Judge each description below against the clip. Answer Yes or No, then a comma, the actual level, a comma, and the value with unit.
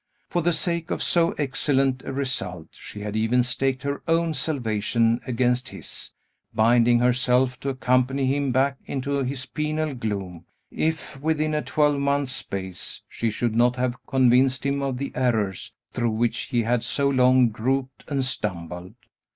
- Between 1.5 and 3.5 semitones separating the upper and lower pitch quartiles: Yes, average, 2.9 semitones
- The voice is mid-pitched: No, low, 130 Hz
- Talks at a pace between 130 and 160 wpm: Yes, average, 155 wpm